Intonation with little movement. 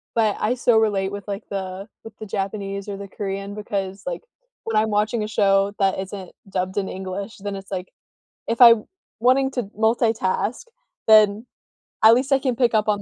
Yes: narrow, 2.3 semitones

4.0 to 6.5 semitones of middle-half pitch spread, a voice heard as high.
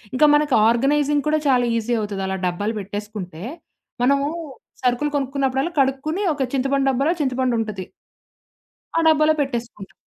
Yes: average, 4.3 semitones; very high, 260 Hz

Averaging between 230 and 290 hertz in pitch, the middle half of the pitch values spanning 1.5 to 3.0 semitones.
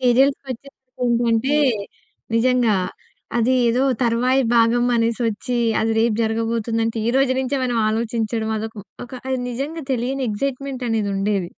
Yes: high, 235 Hz; narrow, 2.4 semitones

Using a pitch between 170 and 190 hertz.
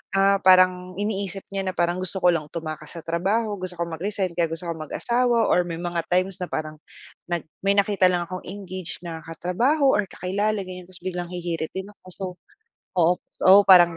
Yes: medium, 185 Hz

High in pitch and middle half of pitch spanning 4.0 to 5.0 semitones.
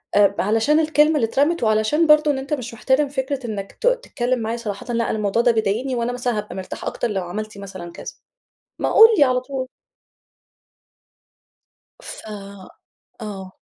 Yes: high, 240 Hz; average, 4.7 semitones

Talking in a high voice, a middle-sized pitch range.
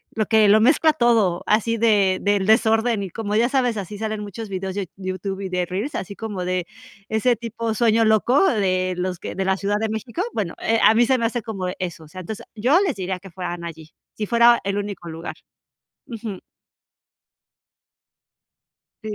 Yes: high, 210 Hz; average, 3.4 semitones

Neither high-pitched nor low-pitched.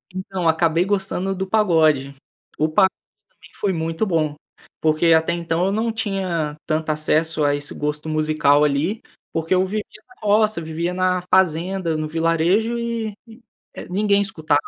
Yes: medium, 170 Hz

